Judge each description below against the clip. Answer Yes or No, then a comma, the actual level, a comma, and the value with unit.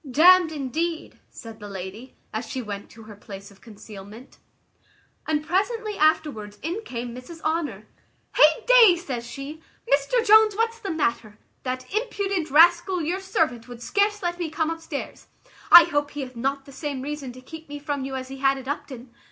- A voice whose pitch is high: Yes, very high, 290 Hz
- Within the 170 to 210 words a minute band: Yes, average, 185 wpm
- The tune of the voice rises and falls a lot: Yes, wide, 5.8 semitones